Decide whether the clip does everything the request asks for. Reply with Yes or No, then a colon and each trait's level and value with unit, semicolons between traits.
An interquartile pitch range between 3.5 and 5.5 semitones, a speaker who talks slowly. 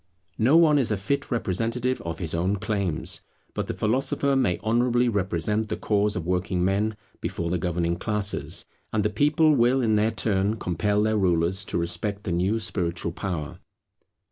No: average, 4.1 semitones; average, 170 wpm